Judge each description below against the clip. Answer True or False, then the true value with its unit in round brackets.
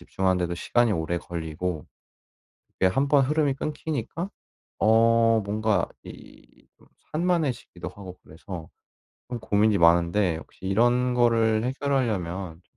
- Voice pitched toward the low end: True (110 Hz)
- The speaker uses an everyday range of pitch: False (5.8 semitones)